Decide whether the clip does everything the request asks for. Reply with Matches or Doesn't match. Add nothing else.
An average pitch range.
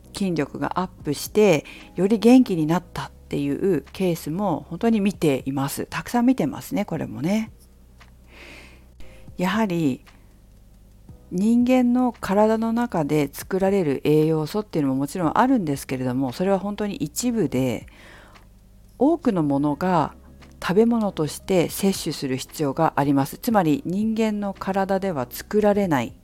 Doesn't match